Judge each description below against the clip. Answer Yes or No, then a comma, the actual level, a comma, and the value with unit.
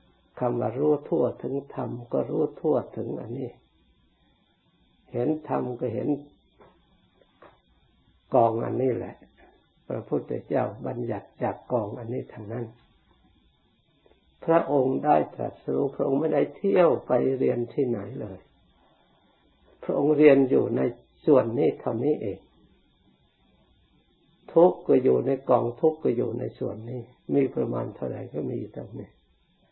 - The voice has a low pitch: Yes, low, 125 Hz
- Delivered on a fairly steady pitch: No, average, 3.2 semitones